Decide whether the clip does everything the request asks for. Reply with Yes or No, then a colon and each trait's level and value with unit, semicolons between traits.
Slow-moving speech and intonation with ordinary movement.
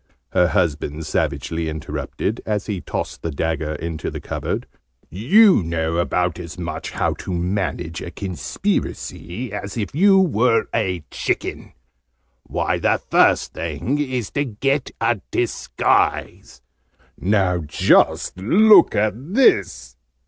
No: slow, 125 wpm; wide, 6.5 semitones